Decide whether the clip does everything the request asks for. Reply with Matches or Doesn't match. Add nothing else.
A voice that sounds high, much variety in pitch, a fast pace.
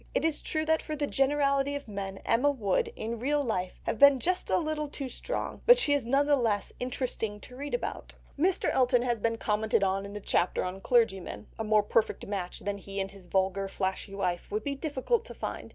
Matches